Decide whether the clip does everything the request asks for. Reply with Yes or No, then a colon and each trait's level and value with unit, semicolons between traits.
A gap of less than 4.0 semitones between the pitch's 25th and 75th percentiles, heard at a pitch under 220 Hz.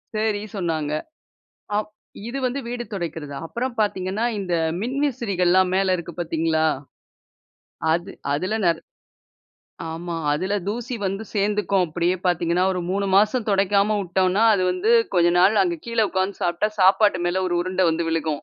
Yes: average, 3.3 semitones; medium, 185 Hz